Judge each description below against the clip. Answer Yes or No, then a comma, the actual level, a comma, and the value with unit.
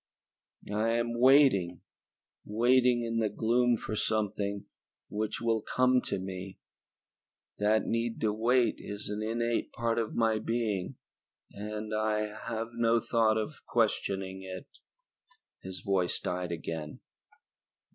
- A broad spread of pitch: No, narrow, 2.5 semitones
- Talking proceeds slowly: Yes, slow, 125 wpm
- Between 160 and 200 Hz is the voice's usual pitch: No, low, 110 Hz